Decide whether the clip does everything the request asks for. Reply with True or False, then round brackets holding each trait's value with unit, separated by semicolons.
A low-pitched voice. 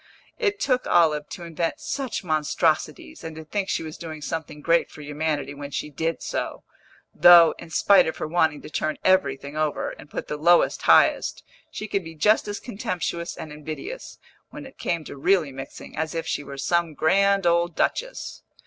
False (165 Hz)